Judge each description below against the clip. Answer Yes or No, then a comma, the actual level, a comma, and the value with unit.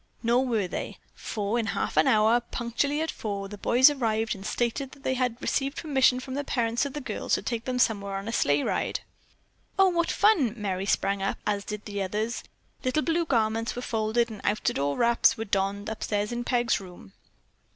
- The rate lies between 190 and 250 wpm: Yes, average, 200 wpm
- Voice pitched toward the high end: Yes, high, 230 Hz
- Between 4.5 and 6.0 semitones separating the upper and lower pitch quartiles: No, average, 3.8 semitones